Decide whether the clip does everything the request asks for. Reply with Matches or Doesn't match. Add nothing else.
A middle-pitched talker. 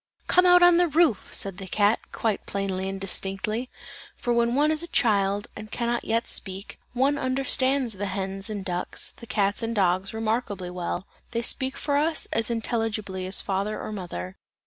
Doesn't match